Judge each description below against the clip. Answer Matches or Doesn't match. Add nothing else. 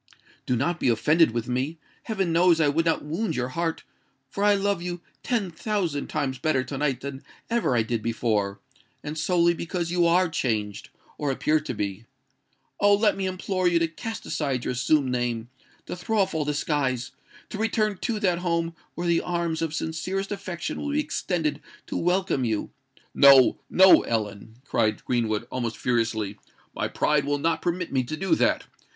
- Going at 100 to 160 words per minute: Doesn't match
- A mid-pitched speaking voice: Matches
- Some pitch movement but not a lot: Doesn't match